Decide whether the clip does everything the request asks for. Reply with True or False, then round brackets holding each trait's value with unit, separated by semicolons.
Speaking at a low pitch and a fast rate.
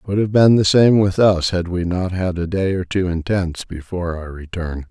True (90 Hz; 255 wpm)